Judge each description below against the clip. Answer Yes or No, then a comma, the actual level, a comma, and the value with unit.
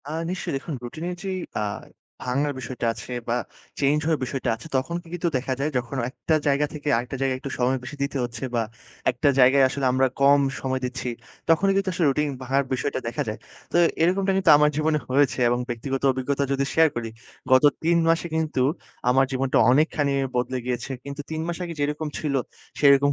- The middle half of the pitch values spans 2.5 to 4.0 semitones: Yes, average, 3.2 semitones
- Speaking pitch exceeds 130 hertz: Yes, medium, 140 Hz